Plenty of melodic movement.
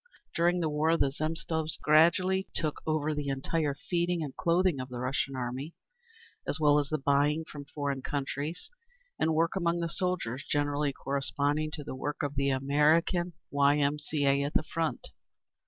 No: narrow, 2.6 semitones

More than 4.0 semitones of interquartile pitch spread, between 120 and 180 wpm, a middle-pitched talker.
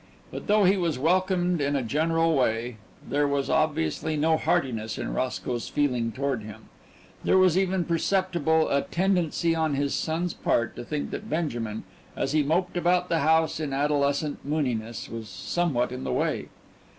Yes: average, 4.7 semitones; average, 165 wpm; medium, 150 Hz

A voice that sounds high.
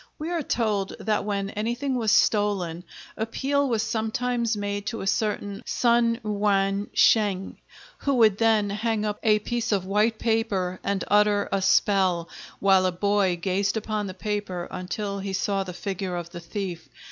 Yes: high, 205 Hz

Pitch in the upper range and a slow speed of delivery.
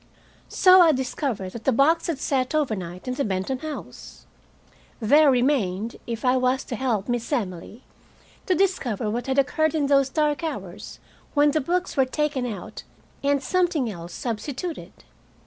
No: very high, 265 Hz; average, 160 wpm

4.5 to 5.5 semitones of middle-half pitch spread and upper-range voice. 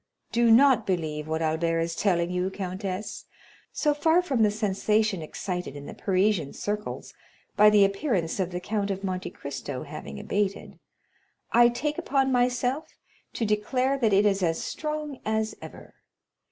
Yes: average, 5.0 semitones; high, 205 Hz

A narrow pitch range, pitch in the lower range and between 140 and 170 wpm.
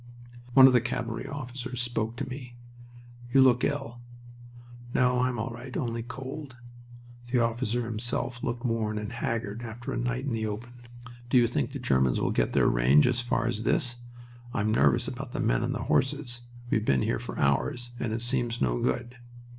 No: narrow, 2.0 semitones; low, 120 Hz; average, 185 wpm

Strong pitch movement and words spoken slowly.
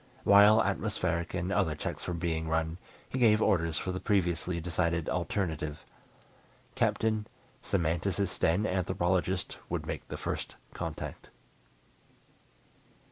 No: average, 3.1 semitones; slow, 115 wpm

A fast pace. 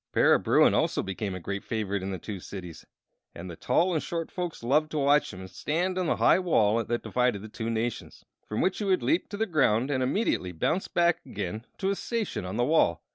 Yes: fast, 230 wpm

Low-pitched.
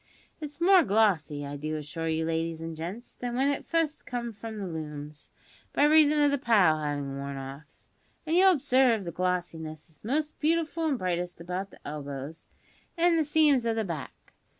No: medium, 185 Hz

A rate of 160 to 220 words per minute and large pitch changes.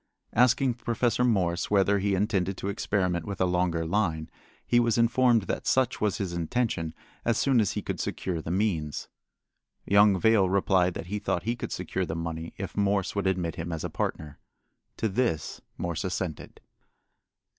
No: average, 175 wpm; average, 4.1 semitones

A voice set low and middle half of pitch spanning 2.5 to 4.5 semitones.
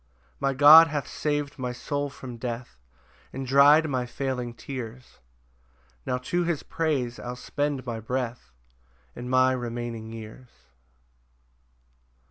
Yes: low, 130 Hz; average, 2.9 semitones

